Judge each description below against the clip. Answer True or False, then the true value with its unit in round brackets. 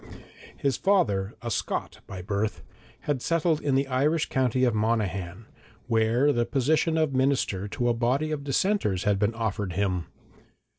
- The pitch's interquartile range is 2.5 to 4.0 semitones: False (5.5 semitones)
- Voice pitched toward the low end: True (120 Hz)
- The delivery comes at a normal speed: True (155 wpm)